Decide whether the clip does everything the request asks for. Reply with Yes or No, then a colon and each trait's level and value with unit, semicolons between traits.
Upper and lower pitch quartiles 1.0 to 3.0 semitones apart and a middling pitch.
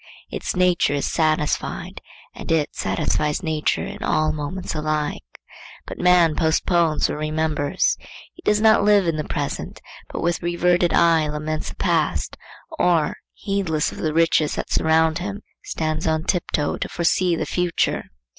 Yes: narrow, 2.4 semitones; medium, 160 Hz